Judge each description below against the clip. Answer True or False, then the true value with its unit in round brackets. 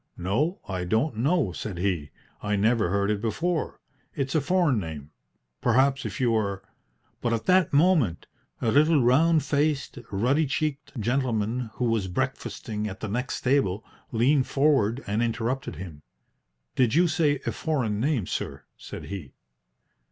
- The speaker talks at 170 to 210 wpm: False (155 wpm)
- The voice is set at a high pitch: False (120 Hz)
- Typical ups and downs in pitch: False (5.9 semitones)